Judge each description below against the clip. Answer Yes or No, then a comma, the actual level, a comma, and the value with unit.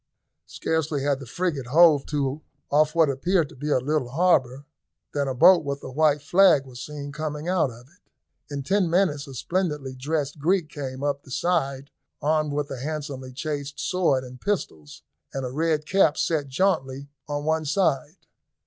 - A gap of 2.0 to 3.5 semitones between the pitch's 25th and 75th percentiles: Yes, average, 2.9 semitones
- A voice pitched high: No, medium, 145 Hz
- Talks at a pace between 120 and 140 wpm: No, average, 175 wpm